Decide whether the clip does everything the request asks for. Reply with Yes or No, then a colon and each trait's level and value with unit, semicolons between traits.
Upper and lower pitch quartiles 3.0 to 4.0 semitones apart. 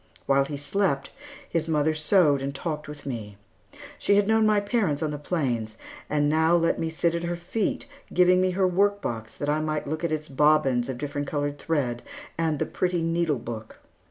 Yes: average, 3.5 semitones